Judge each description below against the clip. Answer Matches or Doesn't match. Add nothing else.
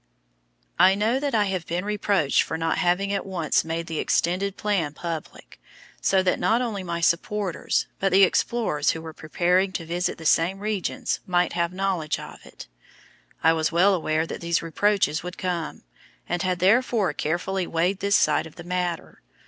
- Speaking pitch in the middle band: Matches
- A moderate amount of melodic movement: Matches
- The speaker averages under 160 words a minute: Doesn't match